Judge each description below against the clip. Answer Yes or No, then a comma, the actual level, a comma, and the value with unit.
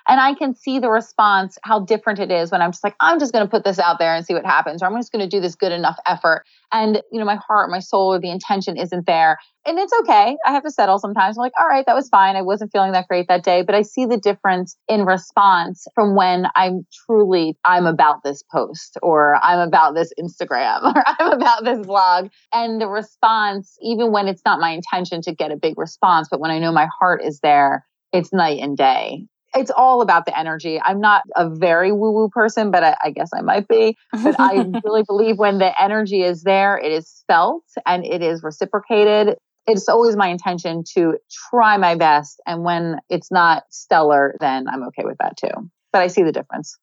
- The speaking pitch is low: No, high, 195 Hz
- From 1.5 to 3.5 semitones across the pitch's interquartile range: No, average, 4.2 semitones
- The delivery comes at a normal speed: No, fast, 230 wpm